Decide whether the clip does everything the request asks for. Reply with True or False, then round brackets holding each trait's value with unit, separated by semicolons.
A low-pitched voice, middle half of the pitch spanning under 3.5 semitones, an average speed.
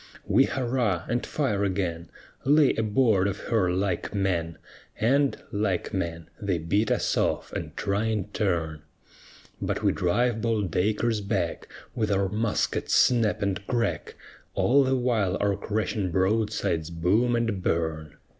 False (100 Hz; 4.1 semitones; 145 wpm)